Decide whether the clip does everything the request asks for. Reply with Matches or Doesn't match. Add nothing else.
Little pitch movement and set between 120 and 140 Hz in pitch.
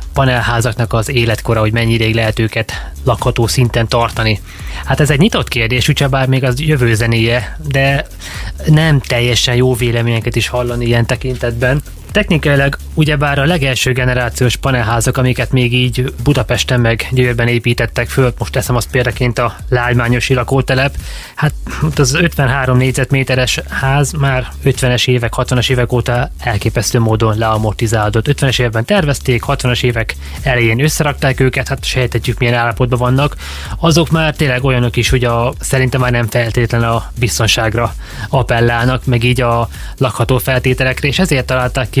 Matches